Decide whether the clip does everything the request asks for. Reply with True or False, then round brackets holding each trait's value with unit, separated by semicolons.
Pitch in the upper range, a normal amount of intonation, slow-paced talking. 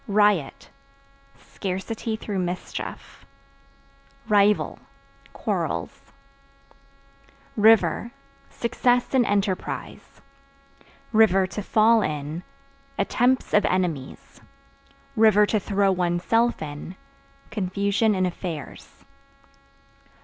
True (200 Hz; 3.3 semitones; 70 wpm)